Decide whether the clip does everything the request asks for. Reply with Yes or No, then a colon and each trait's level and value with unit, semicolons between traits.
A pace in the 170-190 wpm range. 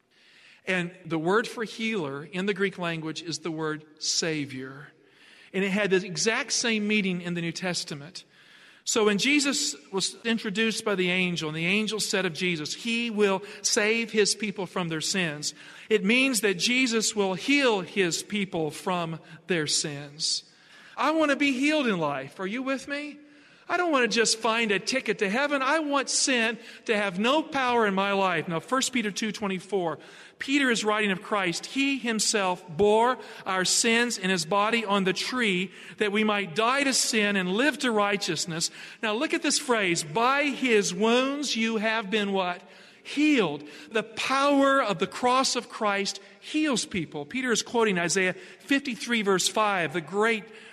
Yes: average, 175 wpm